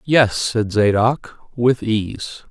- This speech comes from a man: Yes, male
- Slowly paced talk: Yes, slow, 120 wpm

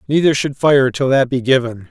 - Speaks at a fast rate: Yes, fast, 220 wpm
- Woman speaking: No, male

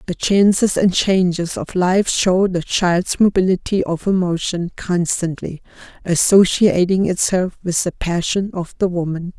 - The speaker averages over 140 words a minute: No, slow, 135 wpm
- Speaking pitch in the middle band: Yes, medium, 180 Hz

